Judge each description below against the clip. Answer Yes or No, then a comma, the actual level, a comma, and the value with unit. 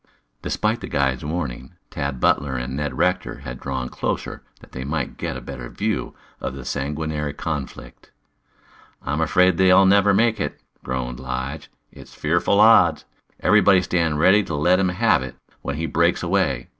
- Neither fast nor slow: Yes, average, 165 wpm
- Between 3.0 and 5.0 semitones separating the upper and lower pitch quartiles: No, wide, 5.4 semitones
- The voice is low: Yes, very low, 75 Hz